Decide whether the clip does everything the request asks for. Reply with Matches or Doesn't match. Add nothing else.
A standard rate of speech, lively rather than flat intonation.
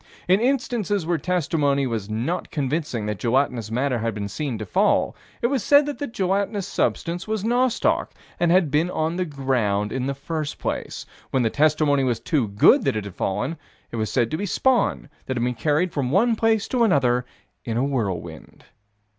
Matches